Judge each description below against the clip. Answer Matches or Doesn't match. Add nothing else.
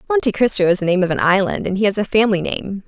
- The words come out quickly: Matches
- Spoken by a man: Doesn't match